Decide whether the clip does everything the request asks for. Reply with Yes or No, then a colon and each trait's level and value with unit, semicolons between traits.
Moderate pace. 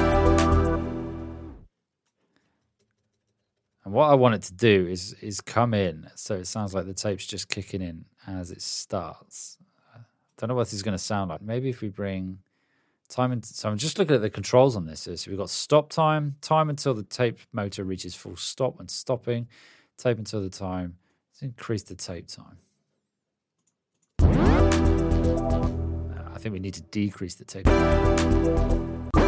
Yes: average, 165 wpm